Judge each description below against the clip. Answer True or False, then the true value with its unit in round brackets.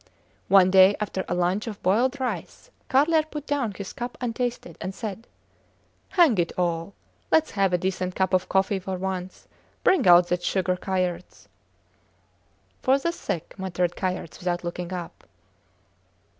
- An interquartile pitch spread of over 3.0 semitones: True (4.8 semitones)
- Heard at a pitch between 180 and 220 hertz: True (190 Hz)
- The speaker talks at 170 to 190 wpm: False (150 wpm)